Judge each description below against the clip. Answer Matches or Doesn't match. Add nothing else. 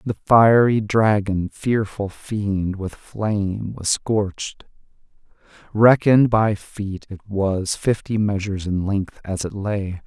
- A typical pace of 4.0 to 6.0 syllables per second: Doesn't match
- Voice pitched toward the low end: Matches